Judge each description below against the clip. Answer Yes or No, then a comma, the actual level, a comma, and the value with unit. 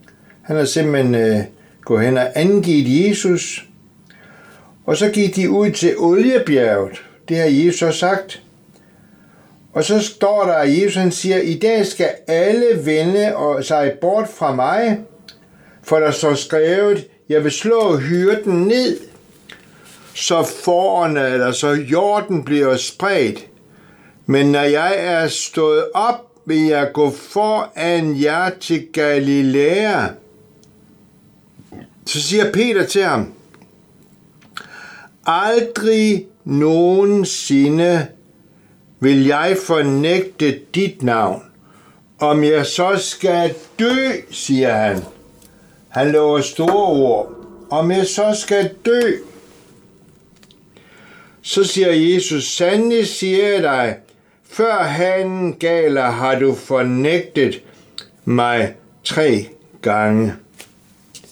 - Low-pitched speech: No, medium, 175 Hz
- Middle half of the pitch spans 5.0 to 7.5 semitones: Yes, wide, 5.5 semitones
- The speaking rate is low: Yes, slow, 110 wpm